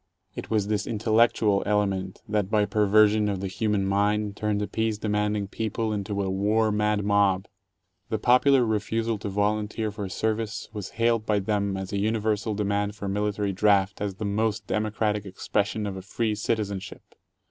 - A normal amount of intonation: No, narrow, 1.2 semitones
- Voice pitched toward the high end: No, low, 105 Hz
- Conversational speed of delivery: Yes, average, 170 wpm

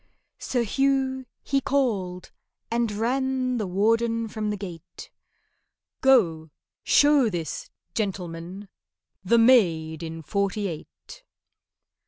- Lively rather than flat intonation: Yes, wide, 6.0 semitones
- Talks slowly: Yes, slow, 95 wpm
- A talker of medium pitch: No, high, 215 Hz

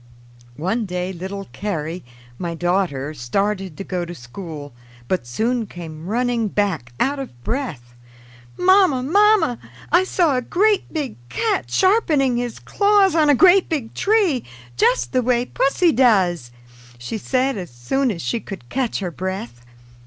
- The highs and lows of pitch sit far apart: Yes, wide, 8.3 semitones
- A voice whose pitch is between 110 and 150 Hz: No, high, 220 Hz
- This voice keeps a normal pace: Yes, average, 150 wpm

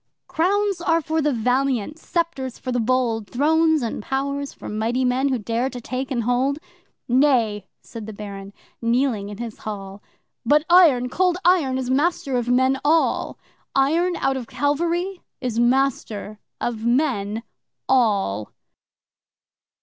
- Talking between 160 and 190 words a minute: No, average, 140 wpm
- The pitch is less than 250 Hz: No, very high, 260 Hz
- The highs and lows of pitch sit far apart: No, average, 4.3 semitones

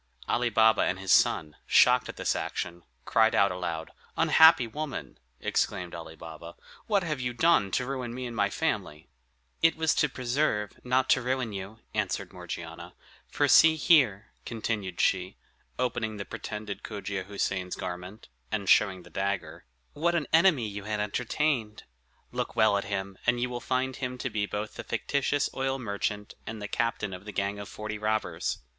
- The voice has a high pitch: No, low, 105 Hz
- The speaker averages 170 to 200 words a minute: Yes, average, 175 wpm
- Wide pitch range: No, average, 4.7 semitones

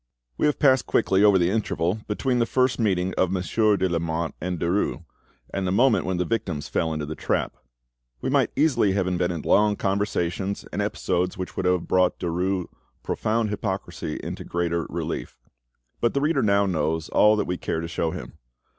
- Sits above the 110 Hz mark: No, very low, 95 Hz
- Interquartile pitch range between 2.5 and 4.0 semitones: Yes, average, 3.4 semitones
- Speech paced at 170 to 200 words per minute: Yes, average, 185 wpm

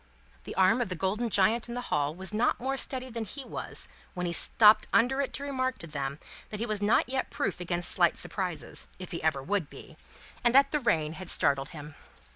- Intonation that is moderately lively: No, wide, 6.5 semitones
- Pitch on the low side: No, high, 200 Hz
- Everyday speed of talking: No, fast, 225 wpm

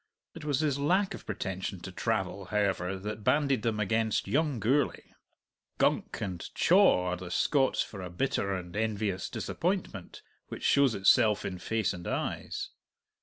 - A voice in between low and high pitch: No, low, 105 Hz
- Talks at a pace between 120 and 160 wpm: Yes, average, 155 wpm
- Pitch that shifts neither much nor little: No, wide, 6.4 semitones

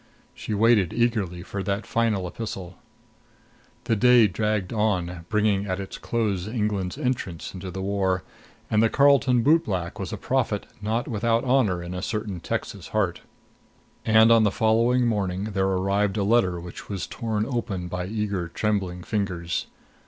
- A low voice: Yes, low, 105 Hz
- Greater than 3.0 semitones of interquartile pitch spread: Yes, average, 3.5 semitones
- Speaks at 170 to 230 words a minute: No, average, 155 wpm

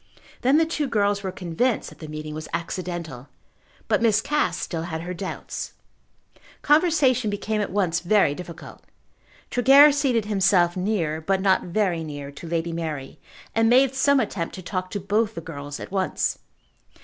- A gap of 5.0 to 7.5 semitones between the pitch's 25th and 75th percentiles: Yes, average, 5.3 semitones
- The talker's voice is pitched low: No, high, 190 Hz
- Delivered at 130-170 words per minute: Yes, average, 165 wpm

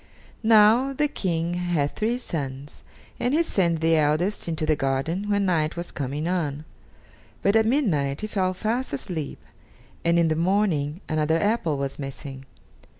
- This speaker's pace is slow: No, average, 155 wpm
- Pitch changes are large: Yes, wide, 5.7 semitones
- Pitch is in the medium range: Yes, medium, 170 Hz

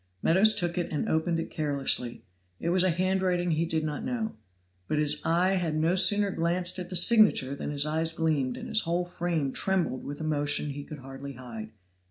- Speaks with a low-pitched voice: No, medium, 165 Hz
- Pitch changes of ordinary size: Yes, average, 3.7 semitones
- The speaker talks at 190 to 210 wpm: Yes, average, 200 wpm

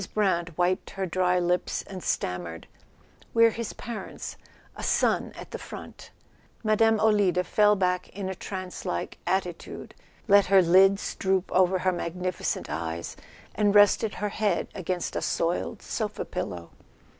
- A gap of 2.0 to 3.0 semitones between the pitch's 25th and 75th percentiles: Yes, narrow, 2.5 semitones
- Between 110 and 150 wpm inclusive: Yes, average, 145 wpm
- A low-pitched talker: No, medium, 185 Hz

